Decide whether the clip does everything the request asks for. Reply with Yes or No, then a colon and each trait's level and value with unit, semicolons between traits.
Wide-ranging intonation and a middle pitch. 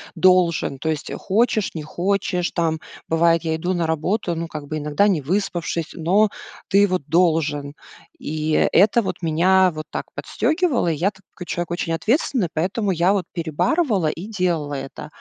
No: average, 3.6 semitones; medium, 175 Hz